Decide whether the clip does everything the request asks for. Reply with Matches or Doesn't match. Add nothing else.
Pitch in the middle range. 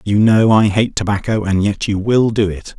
Doesn't match